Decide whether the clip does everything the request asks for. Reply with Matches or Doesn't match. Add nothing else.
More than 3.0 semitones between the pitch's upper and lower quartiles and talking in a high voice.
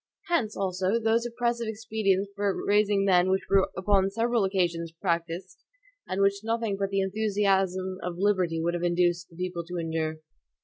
Doesn't match